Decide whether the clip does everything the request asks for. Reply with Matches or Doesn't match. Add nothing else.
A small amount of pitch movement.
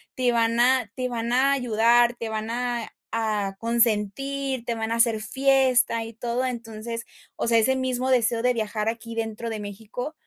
Matches